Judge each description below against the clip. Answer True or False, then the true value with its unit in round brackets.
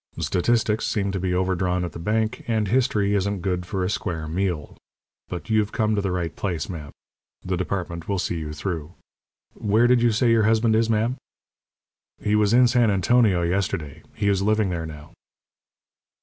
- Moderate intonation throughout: True (3.7 semitones)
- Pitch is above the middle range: False (100 Hz)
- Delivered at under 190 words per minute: True (180 wpm)